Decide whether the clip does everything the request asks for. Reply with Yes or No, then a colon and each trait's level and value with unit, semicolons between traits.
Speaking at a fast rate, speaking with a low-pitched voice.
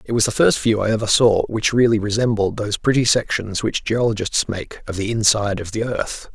Yes: fast, 220 wpm; low, 110 Hz